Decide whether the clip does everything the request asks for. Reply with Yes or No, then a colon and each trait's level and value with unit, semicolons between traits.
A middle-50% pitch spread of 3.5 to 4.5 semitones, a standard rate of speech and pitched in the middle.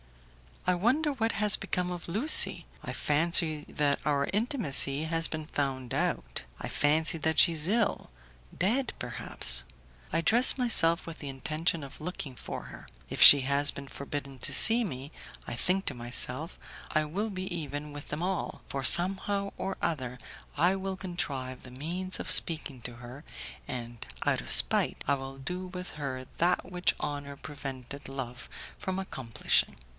No: average, 5.1 semitones; average, 165 wpm; medium, 155 Hz